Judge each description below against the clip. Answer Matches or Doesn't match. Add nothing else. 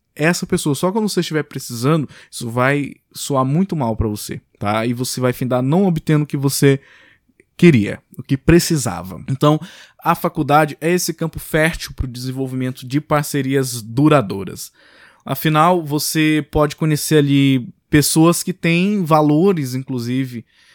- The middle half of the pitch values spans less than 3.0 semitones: Doesn't match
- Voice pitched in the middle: Matches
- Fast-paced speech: Doesn't match